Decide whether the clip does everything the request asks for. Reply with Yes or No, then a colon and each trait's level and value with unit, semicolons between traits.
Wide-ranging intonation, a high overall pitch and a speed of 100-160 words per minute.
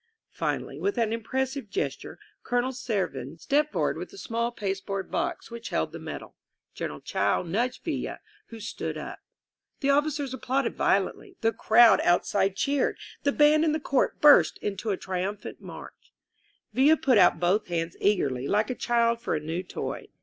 No: wide, 6.0 semitones; high, 230 Hz; average, 170 wpm